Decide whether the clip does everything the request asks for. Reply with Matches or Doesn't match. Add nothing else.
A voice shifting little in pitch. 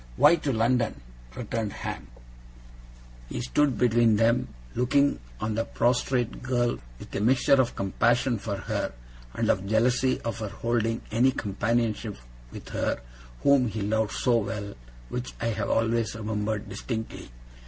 Matches